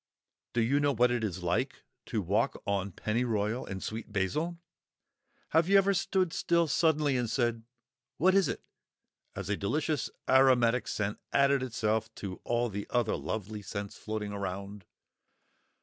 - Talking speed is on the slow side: No, average, 150 wpm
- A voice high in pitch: No, low, 115 Hz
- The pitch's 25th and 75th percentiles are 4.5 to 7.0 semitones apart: Yes, wide, 5.5 semitones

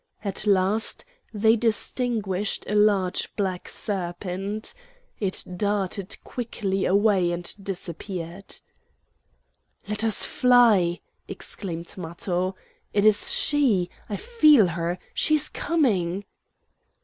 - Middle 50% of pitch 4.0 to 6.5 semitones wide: No, average, 3.3 semitones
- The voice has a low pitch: No, high, 200 Hz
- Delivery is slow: Yes, slow, 100 wpm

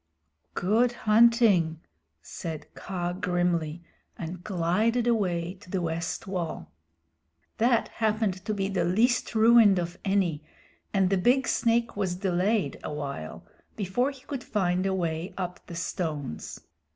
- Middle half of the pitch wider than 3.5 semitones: Yes, average, 4.2 semitones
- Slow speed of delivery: Yes, slow, 130 wpm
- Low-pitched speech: No, medium, 185 Hz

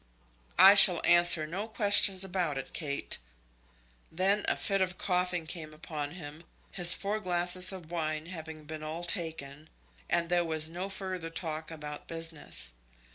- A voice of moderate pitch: Yes, medium, 170 Hz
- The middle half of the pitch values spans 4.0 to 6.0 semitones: No, average, 2.9 semitones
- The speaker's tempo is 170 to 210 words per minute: No, average, 150 wpm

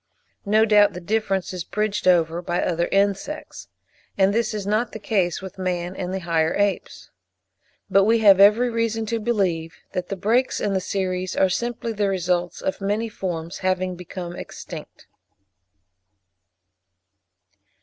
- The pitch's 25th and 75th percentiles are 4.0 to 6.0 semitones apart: No, average, 3.0 semitones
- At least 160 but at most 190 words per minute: No, average, 150 wpm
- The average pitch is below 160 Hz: No, high, 195 Hz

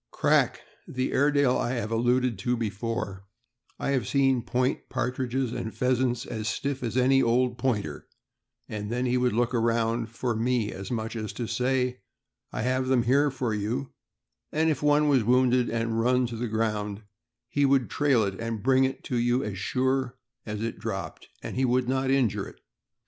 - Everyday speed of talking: Yes, average, 180 wpm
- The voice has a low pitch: Yes, low, 125 Hz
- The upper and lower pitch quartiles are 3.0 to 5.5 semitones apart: No, narrow, 2.4 semitones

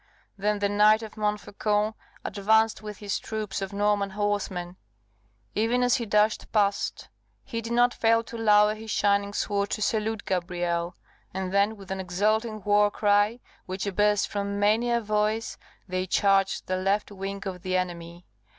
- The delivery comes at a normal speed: Yes, average, 160 wpm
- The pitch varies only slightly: Yes, narrow, 1.8 semitones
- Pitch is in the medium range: No, high, 205 Hz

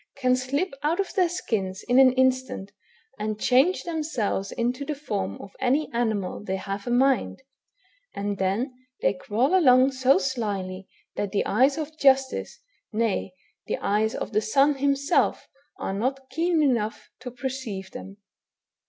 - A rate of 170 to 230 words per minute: No, average, 155 wpm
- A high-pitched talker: Yes, very high, 255 Hz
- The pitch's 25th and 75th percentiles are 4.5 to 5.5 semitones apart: Yes, average, 5.0 semitones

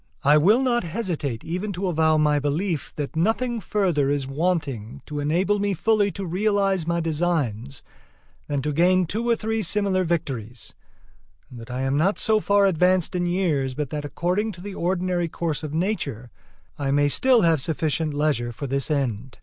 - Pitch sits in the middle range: Yes, medium, 165 Hz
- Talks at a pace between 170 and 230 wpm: Yes, average, 180 wpm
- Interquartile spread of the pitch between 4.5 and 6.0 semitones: Yes, average, 5.1 semitones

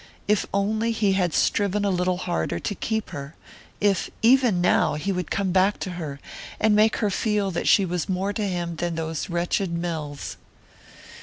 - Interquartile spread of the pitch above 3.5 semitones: No, average, 3.1 semitones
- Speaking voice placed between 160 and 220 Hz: Yes, medium, 185 Hz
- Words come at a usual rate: Yes, average, 180 wpm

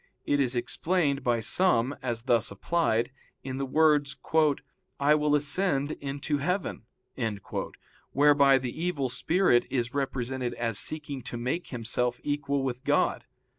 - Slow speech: Yes, slow, 130 wpm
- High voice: No, low, 135 Hz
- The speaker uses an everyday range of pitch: Yes, average, 3.2 semitones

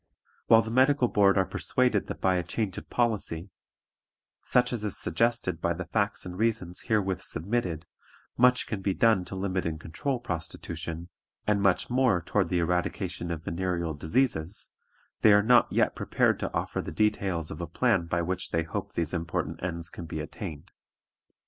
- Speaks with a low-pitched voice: Yes, very low, 95 Hz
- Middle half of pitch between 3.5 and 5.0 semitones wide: Yes, average, 4.6 semitones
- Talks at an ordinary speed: Yes, average, 175 wpm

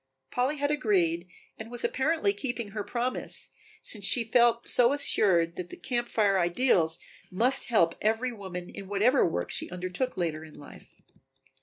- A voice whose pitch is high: Yes, high, 215 Hz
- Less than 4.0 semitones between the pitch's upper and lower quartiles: No, wide, 5.6 semitones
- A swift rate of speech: No, average, 160 wpm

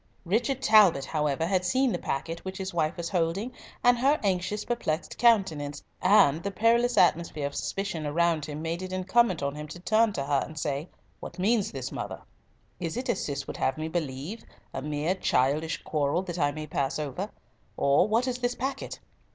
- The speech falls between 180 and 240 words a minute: Yes, average, 190 wpm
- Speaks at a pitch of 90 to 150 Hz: No, medium, 170 Hz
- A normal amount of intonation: No, wide, 5.7 semitones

